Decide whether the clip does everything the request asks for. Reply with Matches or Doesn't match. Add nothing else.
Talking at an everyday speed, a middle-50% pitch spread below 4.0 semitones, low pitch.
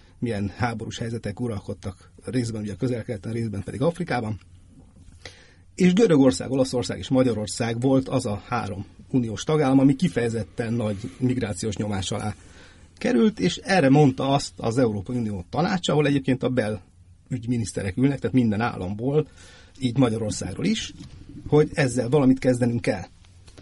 Doesn't match